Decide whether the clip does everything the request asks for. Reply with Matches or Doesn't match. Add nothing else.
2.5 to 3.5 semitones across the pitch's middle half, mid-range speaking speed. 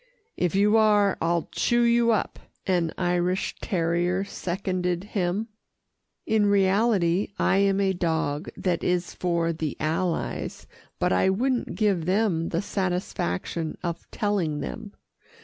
Doesn't match